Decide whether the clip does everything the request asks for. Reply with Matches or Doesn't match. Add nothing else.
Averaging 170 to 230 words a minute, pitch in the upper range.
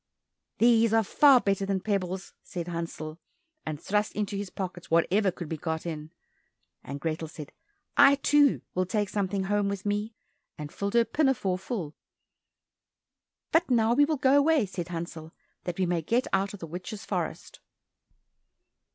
Doesn't match